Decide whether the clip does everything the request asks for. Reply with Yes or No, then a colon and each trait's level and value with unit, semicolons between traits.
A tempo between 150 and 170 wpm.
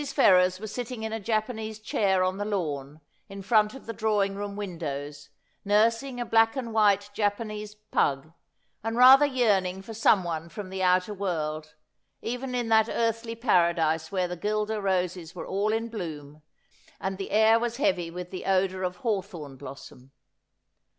Yes: average, 165 wpm